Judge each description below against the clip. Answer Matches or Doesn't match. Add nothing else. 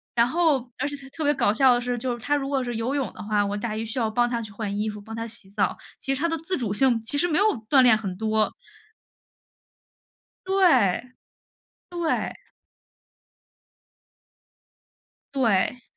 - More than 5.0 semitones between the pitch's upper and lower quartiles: Doesn't match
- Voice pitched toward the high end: Matches